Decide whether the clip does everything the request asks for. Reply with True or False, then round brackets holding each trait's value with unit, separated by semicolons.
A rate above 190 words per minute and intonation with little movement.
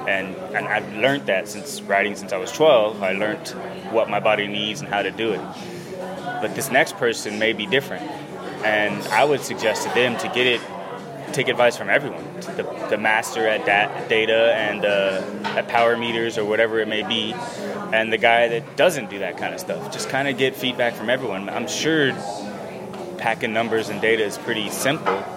True (200 wpm; 2.0 semitones)